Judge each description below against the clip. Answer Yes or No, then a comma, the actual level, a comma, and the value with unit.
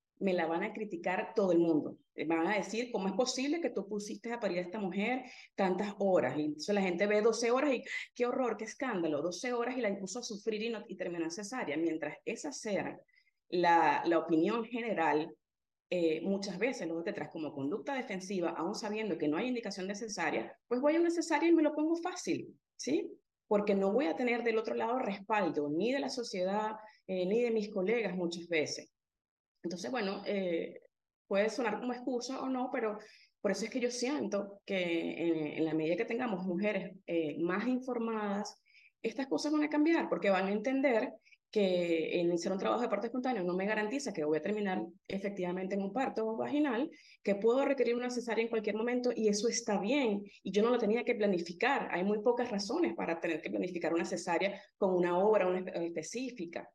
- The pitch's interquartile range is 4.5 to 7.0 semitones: Yes, average, 5.3 semitones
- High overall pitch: Yes, high, 210 Hz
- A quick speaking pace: Yes, fast, 205 wpm